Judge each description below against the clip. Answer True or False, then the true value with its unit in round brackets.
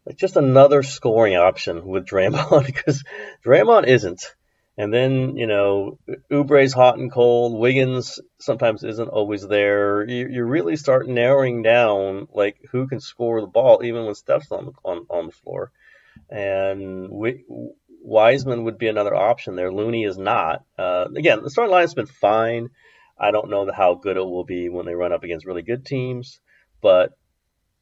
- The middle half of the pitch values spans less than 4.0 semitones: False (4.3 semitones)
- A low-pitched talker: True (115 Hz)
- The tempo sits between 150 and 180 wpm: True (175 wpm)